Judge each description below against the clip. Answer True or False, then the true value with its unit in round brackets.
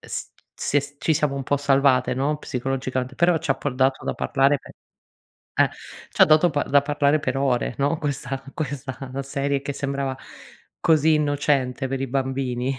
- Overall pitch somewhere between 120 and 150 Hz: True (140 Hz)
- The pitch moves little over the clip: True (1.5 semitones)